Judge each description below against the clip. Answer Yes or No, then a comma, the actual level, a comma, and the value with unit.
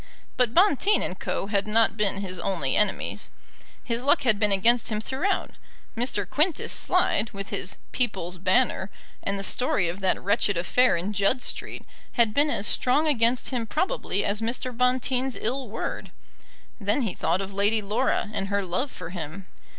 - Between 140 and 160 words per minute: No, average, 175 wpm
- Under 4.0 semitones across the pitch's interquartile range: No, average, 4.3 semitones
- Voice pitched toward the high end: Yes, high, 215 Hz